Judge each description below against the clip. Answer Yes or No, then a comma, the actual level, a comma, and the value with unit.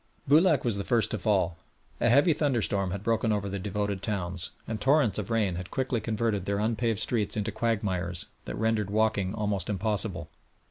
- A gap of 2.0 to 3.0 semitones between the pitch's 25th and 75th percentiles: Yes, average, 2.7 semitones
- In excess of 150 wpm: Yes, average, 180 wpm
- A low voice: Yes, low, 105 Hz